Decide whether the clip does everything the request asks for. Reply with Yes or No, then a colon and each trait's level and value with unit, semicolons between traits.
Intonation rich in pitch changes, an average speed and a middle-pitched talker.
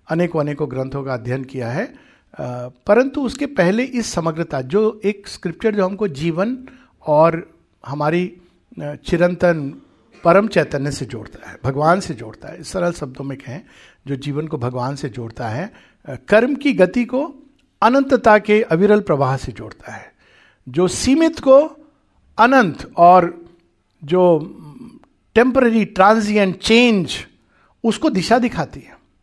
Yes: wide, 7.5 semitones; average, 135 wpm; medium, 175 Hz